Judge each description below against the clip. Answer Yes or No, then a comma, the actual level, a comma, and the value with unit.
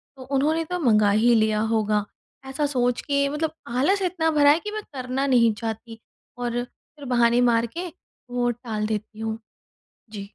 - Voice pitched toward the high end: Yes, high, 245 Hz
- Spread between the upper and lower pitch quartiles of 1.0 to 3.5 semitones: No, average, 4.4 semitones